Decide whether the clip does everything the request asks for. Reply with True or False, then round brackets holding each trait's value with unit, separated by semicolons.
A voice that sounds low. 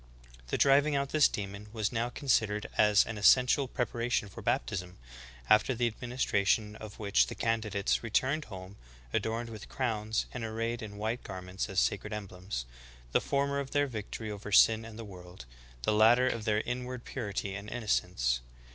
True (110 Hz)